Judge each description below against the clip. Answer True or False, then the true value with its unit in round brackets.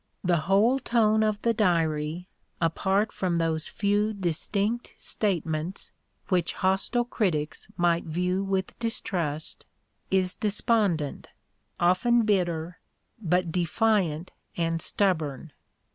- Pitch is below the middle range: False (185 Hz)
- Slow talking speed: True (100 wpm)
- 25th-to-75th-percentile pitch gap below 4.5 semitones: True (4.0 semitones)